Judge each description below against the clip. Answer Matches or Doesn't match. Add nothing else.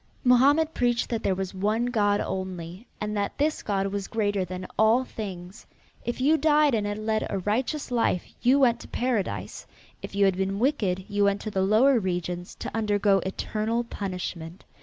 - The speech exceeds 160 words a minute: Matches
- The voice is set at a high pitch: Matches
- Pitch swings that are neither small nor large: Matches